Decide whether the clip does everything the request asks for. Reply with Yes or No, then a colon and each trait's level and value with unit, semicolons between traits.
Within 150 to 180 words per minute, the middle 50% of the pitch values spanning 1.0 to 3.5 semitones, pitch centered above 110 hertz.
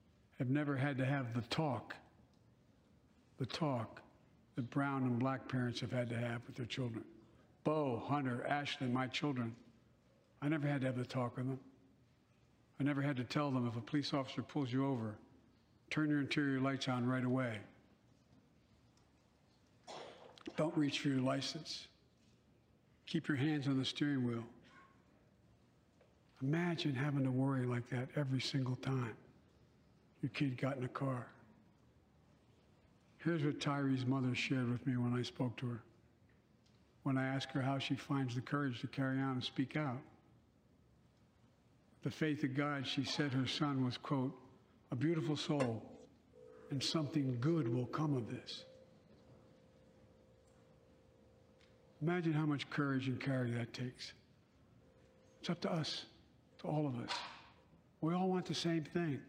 Yes: average, 155 wpm; average, 2.8 semitones; low, 135 Hz